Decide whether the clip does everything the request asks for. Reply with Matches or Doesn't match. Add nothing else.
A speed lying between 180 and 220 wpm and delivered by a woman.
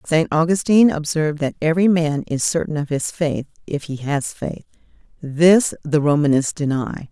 Doesn't match